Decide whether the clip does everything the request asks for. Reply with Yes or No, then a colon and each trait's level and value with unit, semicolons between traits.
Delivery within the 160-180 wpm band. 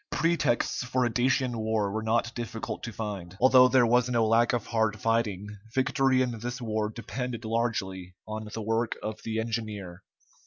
Yes: average, 170 wpm